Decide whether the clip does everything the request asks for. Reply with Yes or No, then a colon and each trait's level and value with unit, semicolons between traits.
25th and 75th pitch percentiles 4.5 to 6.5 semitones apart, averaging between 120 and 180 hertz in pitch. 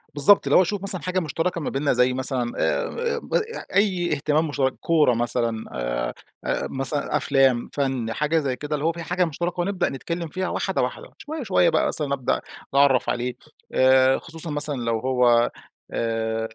Yes: average, 5.2 semitones; medium, 140 Hz